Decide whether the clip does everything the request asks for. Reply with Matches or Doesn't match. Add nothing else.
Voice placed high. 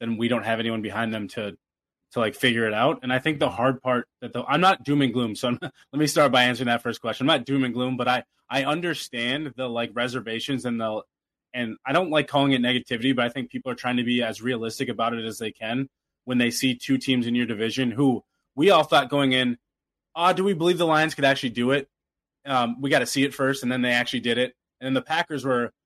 Doesn't match